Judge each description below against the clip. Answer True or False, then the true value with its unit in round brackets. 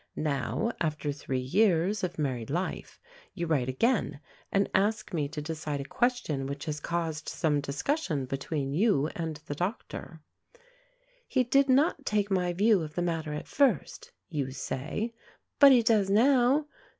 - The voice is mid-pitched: True (170 Hz)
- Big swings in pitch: True (6.9 semitones)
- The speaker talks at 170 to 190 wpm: False (155 wpm)